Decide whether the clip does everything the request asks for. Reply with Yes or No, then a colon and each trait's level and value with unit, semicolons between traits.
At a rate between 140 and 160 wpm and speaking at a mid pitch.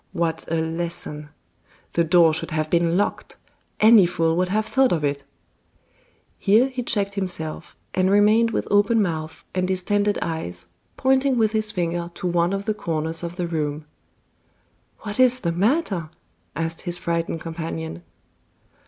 Yes: average, 155 wpm; medium, 175 Hz